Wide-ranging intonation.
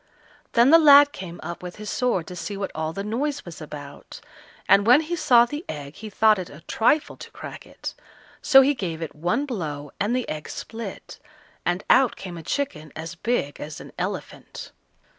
Yes: wide, 7.7 semitones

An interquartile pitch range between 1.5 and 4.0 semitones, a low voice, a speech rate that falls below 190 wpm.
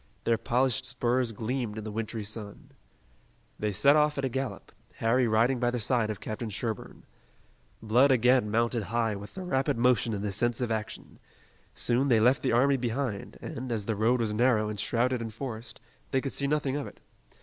No: average, 2.9 semitones; low, 120 Hz; average, 195 wpm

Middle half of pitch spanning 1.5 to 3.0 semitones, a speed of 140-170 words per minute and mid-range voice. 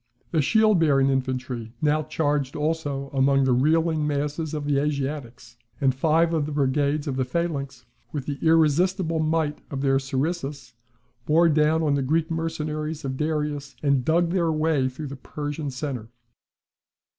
Yes: average, 2.7 semitones; average, 155 wpm; medium, 150 Hz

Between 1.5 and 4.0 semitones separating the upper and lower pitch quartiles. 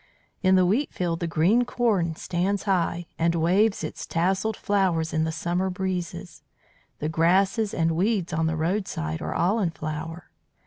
Yes: average, 3.1 semitones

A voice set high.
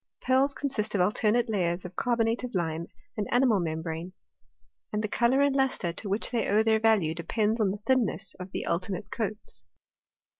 Yes: high, 210 Hz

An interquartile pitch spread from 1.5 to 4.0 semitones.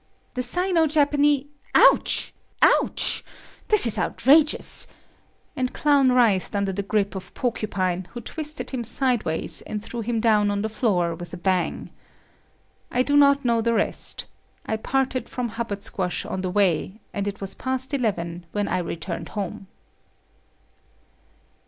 No: average, 5.2 semitones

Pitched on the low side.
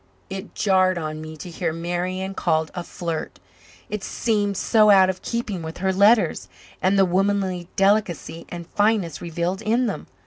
No: medium, 185 Hz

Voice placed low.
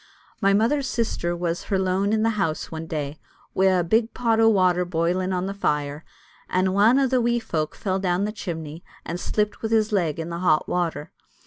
No: medium, 185 Hz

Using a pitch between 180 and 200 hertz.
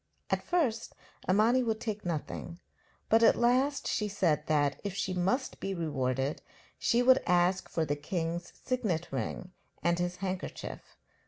Yes: medium, 185 Hz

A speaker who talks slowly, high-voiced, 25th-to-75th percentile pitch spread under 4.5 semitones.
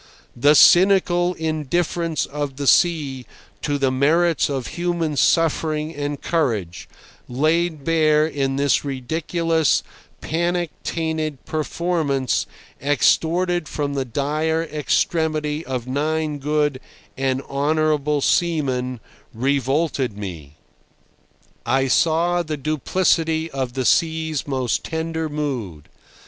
No: slow, 105 wpm; medium, 150 Hz; average, 3.1 semitones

